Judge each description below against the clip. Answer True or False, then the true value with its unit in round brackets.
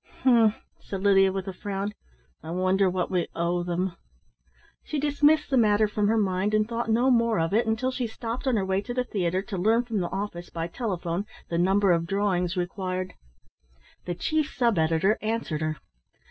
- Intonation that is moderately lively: True (4.0 semitones)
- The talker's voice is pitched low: False (200 Hz)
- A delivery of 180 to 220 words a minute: True (190 wpm)